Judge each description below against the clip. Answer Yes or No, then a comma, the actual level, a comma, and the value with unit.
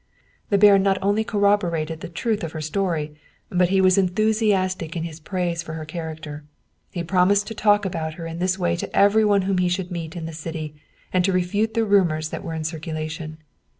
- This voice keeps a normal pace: No, fast, 210 wpm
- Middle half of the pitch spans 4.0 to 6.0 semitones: No, average, 3.6 semitones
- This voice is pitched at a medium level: Yes, medium, 180 Hz